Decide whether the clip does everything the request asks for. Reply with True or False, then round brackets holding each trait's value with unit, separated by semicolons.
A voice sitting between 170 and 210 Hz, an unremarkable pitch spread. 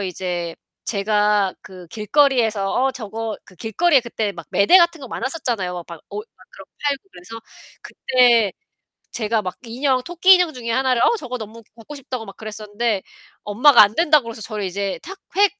False (230 Hz; 4.7 semitones)